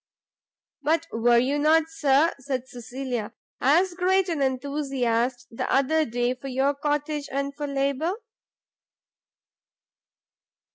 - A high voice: Yes, very high, 275 Hz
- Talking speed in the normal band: No, slow, 110 wpm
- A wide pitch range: No, average, 3.2 semitones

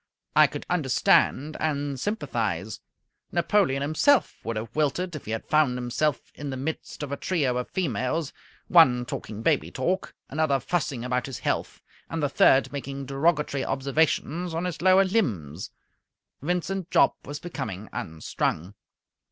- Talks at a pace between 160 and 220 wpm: No, average, 145 wpm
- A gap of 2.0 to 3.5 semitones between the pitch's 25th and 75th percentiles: No, average, 4.7 semitones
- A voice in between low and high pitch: Yes, medium, 145 Hz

